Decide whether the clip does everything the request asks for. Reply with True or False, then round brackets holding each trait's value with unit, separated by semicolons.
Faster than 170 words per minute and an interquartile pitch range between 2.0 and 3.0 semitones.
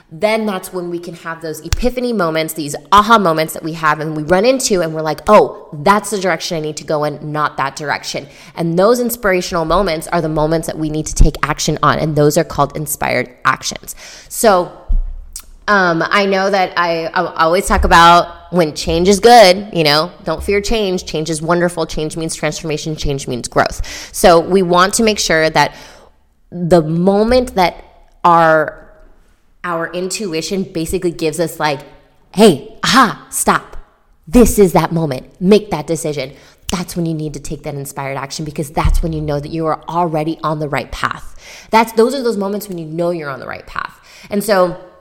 False (195 wpm; 3.4 semitones)